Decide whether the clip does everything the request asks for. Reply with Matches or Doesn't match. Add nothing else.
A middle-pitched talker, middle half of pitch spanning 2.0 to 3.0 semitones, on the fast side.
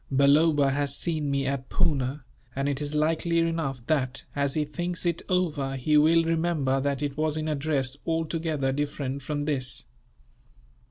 Doesn't match